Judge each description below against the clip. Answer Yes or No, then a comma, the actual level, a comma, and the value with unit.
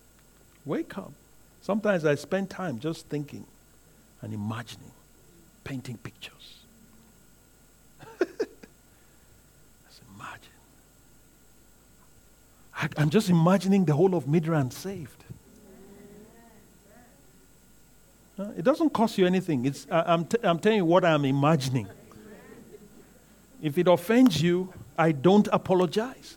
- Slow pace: Yes, slow, 100 wpm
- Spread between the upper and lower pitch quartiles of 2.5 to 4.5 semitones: No, average, 5.3 semitones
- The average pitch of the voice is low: No, medium, 180 Hz